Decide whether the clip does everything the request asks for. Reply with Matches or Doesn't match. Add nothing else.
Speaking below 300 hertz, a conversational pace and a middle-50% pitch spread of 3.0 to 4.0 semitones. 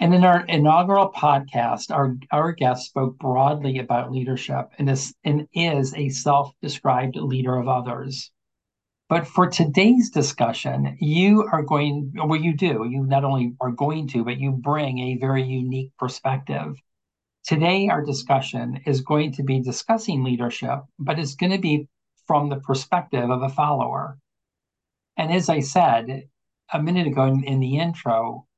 Matches